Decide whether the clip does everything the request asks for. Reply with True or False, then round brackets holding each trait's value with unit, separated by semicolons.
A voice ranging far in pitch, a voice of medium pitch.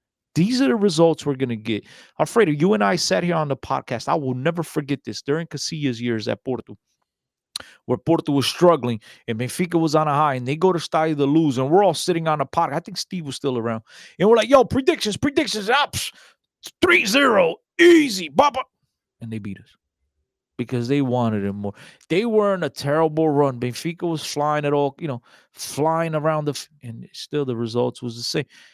True (5.7 semitones; 150 Hz)